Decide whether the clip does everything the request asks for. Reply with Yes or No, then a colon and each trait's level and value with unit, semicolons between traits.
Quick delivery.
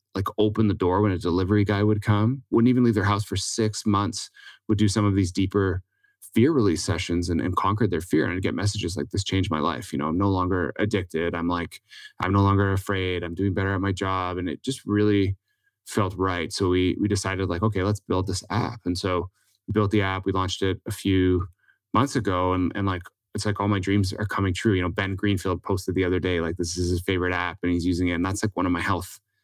Yes: fast, 255 wpm